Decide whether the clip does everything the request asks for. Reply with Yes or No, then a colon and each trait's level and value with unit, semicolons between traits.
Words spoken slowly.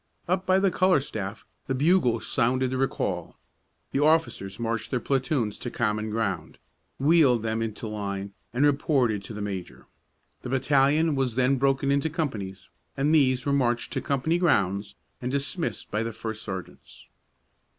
No: average, 160 wpm